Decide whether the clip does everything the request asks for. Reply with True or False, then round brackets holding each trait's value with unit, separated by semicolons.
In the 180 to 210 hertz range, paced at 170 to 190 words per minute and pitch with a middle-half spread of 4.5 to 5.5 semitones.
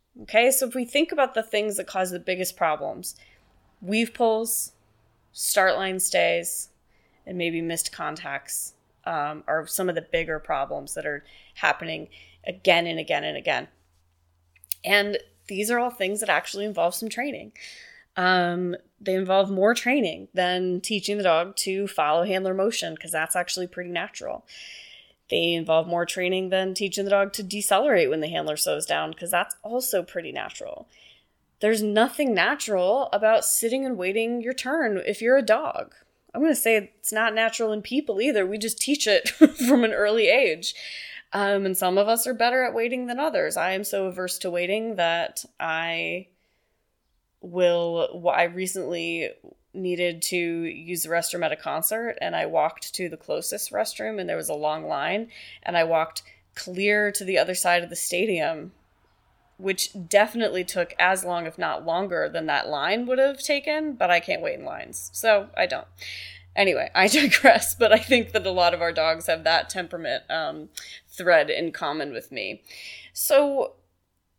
True (190 Hz; 175 wpm; 4.8 semitones)